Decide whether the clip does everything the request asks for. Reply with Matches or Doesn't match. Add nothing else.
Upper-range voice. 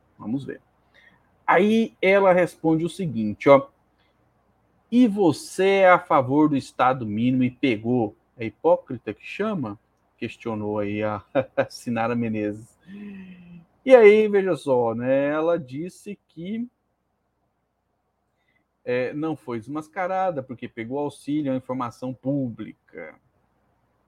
Doesn't match